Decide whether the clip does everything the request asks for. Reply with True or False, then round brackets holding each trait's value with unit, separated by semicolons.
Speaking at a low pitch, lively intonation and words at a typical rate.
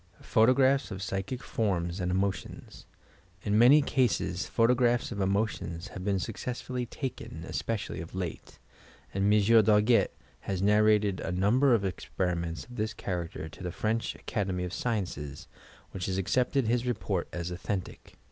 False (100 Hz; 4.2 semitones; 145 wpm)